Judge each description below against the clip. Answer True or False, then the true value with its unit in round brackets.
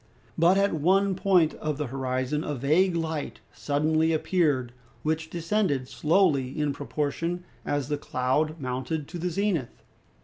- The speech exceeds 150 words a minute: False (140 wpm)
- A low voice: False (155 Hz)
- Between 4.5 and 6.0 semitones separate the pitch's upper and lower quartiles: False (3.6 semitones)